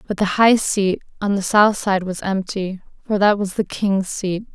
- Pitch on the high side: Yes, high, 200 Hz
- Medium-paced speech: No, fast, 210 wpm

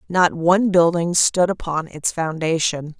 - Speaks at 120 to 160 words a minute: Yes, average, 140 wpm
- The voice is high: No, medium, 170 Hz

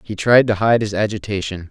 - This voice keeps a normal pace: No, fast, 210 wpm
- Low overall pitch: Yes, low, 105 Hz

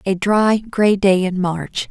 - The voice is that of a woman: Yes, female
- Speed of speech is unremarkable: Yes, average, 190 wpm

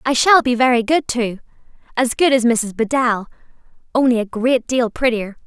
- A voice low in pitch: No, high, 240 Hz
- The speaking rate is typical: Yes, average, 175 wpm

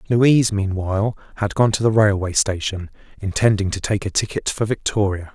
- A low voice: Yes, low, 105 Hz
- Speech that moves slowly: No, average, 170 wpm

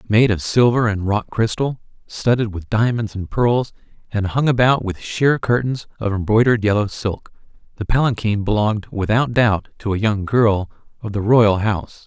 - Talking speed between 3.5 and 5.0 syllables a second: Yes, 4.9 syllables/s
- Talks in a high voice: No, low, 110 Hz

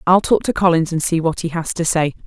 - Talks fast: Yes, fast, 290 wpm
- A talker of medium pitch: Yes, medium, 170 Hz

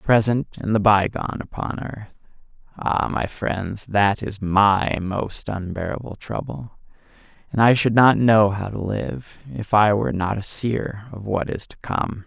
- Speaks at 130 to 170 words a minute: Yes, average, 160 wpm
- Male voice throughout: Yes, male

